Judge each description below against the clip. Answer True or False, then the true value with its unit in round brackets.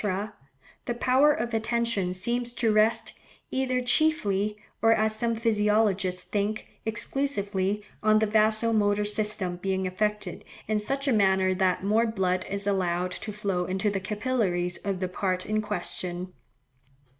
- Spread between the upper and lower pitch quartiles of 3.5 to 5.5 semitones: False (3.0 semitones)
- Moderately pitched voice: False (210 Hz)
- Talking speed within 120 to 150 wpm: True (145 wpm)